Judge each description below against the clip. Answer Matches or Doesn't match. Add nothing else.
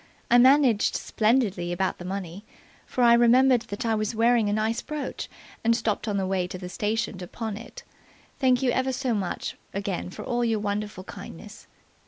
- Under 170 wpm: Doesn't match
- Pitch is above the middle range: Matches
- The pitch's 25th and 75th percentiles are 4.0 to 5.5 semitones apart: Doesn't match